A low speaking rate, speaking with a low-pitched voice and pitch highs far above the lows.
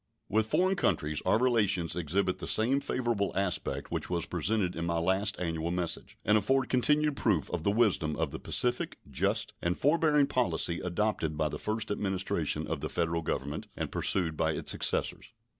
No: average, 175 wpm; very low, 95 Hz; wide, 5.9 semitones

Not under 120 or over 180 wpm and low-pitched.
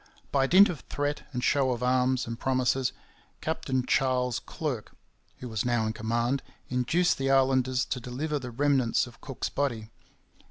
Yes: average, 160 wpm; low, 130 Hz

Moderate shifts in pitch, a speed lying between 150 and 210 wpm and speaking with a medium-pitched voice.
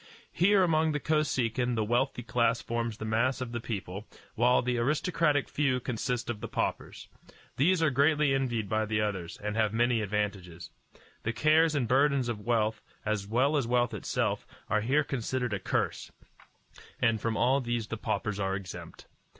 No: average, 3.9 semitones; average, 175 wpm; low, 120 Hz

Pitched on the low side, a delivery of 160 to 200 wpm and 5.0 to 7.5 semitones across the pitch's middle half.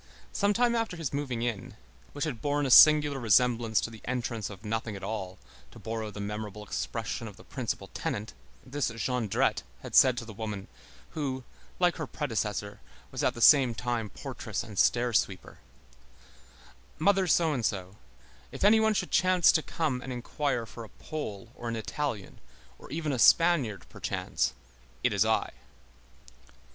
Yes: low, 120 Hz; average, 170 wpm; wide, 5.4 semitones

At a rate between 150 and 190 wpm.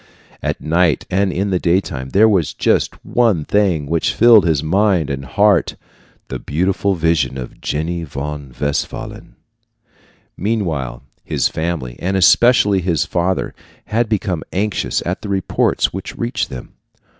No: average, 140 wpm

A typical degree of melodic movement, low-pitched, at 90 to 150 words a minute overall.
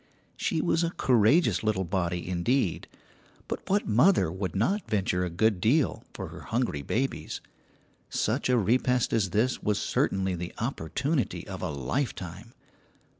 No: wide, 6.0 semitones; low, 110 Hz; average, 145 wpm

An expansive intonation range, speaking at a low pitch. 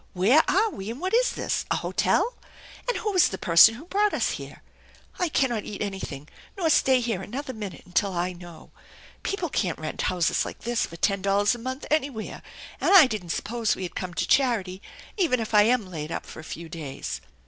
No: wide, 7.1 semitones; high, 215 Hz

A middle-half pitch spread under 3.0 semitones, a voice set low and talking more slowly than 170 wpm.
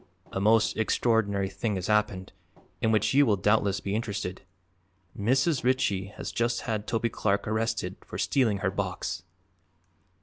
Yes: narrow, 2.5 semitones; low, 105 Hz; average, 145 wpm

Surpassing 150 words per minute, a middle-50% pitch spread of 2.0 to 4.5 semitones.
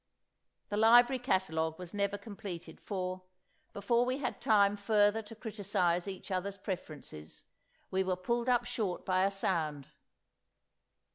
No: slow, 135 wpm; average, 3.3 semitones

